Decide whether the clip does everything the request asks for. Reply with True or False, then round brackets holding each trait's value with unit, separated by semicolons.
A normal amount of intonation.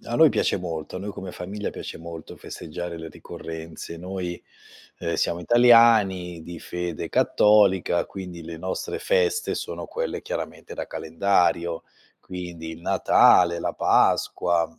True (3.0 semitones)